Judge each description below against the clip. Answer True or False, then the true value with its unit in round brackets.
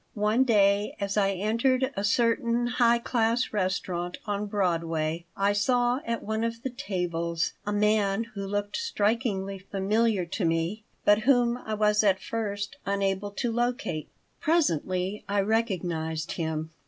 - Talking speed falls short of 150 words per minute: True (140 wpm)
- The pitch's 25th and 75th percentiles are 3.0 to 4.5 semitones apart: True (3.4 semitones)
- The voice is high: True (205 Hz)